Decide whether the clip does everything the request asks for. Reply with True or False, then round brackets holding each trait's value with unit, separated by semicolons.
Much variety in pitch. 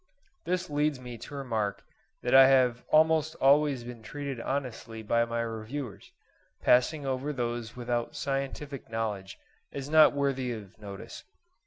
False (3.5 semitones)